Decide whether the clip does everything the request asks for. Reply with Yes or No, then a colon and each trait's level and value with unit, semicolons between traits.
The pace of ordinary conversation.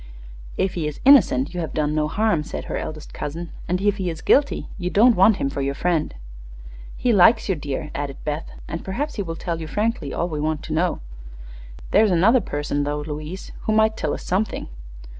No: fast, 210 wpm